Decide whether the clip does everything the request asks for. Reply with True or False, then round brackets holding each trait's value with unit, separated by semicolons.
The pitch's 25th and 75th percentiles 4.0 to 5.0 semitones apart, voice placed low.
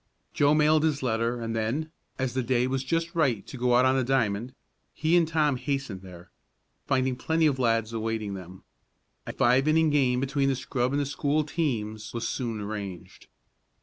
True (4.3 semitones; 130 Hz)